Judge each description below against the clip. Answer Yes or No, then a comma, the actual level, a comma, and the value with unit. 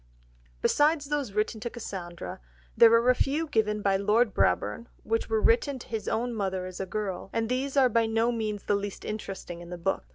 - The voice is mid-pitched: No, high, 220 Hz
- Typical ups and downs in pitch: Yes, average, 3.4 semitones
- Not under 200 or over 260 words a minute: Yes, fast, 205 wpm